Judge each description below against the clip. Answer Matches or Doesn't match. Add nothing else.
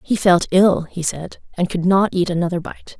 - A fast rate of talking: Matches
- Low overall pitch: Doesn't match